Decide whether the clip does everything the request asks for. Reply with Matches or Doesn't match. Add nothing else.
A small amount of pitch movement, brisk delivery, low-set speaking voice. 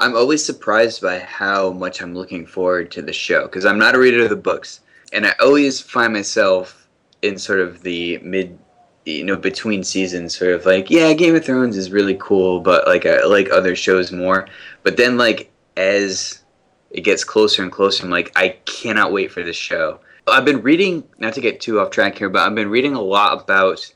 Matches